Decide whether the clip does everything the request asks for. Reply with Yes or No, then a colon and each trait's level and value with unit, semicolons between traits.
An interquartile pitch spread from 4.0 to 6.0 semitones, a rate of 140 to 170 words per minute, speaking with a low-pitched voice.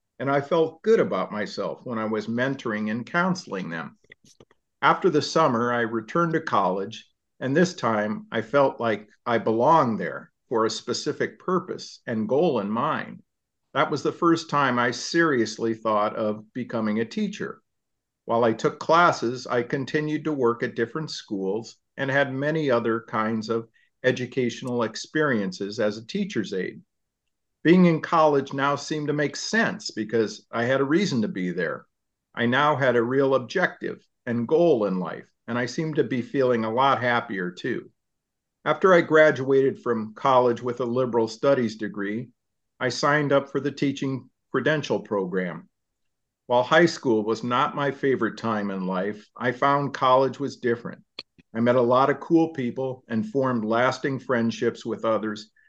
Yes: average, 4.4 semitones; average, 165 wpm; low, 125 Hz